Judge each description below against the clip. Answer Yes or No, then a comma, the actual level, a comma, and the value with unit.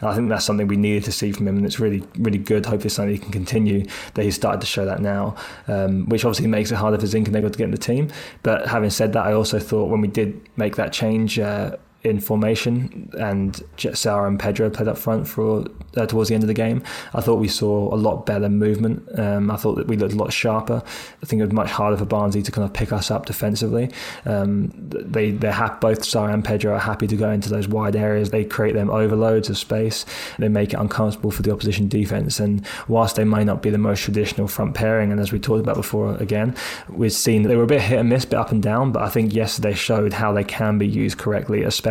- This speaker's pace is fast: Yes, fast, 255 wpm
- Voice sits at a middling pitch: No, low, 105 Hz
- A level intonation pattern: Yes, narrow, 1.3 semitones